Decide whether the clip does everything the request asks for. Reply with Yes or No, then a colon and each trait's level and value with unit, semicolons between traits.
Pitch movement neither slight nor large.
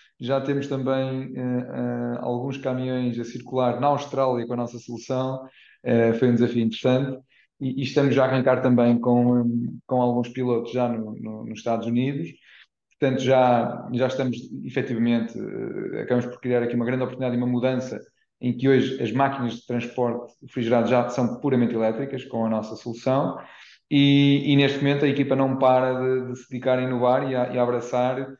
No: narrow, 1.5 semitones